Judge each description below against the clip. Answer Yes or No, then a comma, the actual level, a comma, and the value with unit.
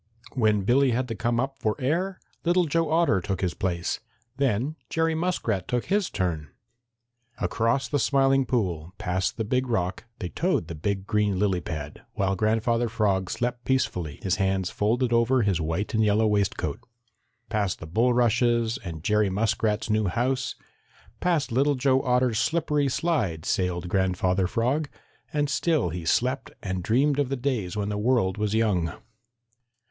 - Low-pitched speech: Yes, low, 110 Hz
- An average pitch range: No, wide, 5.7 semitones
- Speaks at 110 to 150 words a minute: No, average, 160 wpm